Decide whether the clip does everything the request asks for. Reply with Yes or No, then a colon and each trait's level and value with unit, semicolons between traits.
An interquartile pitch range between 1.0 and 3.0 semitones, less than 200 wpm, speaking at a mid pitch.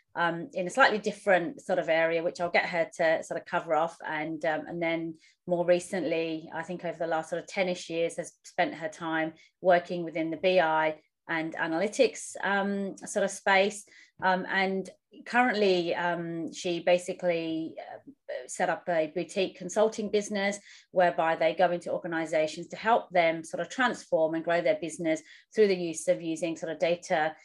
Yes: narrow, 2.6 semitones; average, 175 wpm; medium, 175 Hz